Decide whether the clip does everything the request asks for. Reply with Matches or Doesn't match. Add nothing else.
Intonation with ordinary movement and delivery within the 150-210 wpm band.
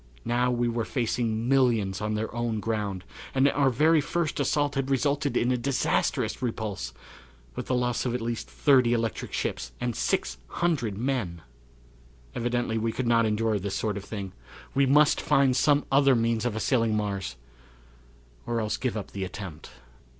Matches